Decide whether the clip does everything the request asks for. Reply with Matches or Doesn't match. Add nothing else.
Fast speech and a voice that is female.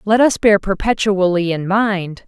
Doesn't match